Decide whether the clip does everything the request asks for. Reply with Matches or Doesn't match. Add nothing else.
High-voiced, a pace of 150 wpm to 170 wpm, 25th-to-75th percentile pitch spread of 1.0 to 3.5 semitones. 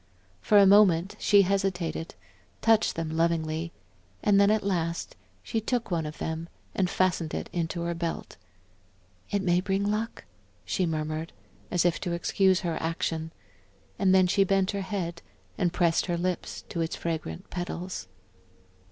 Doesn't match